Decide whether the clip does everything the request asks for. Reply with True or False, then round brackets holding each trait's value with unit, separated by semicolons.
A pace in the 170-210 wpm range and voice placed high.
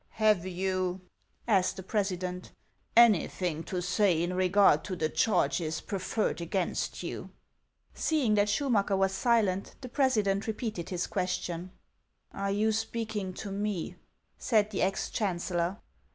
False (150 wpm; 195 Hz)